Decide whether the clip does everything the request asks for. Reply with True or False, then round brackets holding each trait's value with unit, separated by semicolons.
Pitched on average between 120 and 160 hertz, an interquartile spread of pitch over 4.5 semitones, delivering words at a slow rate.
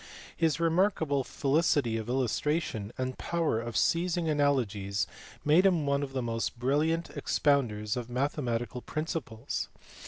True (140 Hz; 5.3 semitones; 125 wpm)